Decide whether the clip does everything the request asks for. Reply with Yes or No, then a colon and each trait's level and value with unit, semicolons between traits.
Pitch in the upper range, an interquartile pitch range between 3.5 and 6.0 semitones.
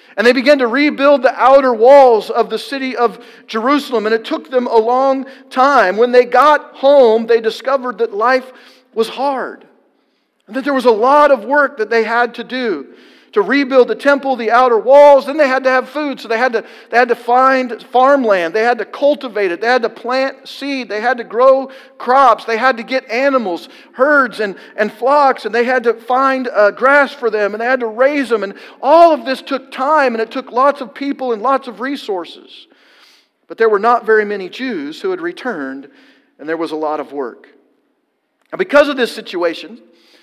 No: very high, 255 Hz; average, 3.1 semitones